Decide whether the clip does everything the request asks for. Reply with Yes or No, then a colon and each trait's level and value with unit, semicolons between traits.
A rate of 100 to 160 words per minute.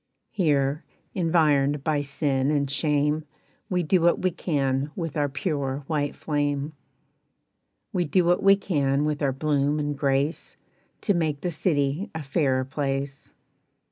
Yes: average, 140 wpm